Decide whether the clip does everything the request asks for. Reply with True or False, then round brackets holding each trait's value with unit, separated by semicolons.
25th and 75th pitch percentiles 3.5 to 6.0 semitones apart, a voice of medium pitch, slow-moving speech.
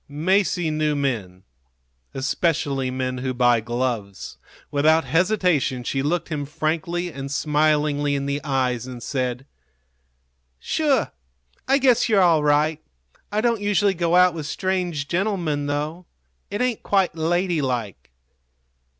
True (4.9 semitones; 150 Hz; 125 wpm)